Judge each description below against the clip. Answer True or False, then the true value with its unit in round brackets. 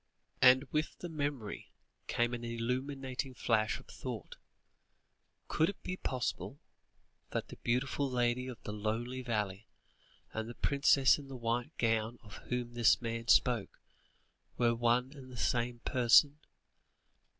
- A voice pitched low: True (120 Hz)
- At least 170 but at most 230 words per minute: False (140 wpm)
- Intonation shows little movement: True (2.3 semitones)